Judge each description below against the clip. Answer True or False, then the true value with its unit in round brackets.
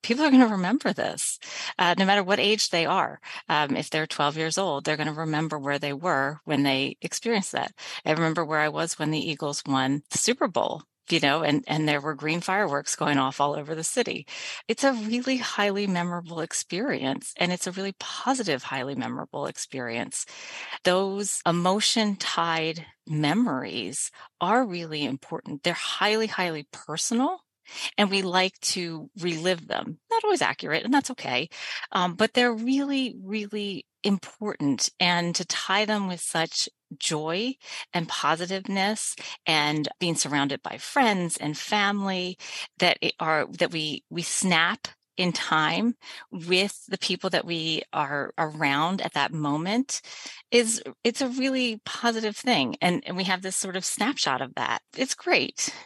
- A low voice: False (180 Hz)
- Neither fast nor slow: True (165 wpm)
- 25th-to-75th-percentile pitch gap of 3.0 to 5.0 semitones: False (5.5 semitones)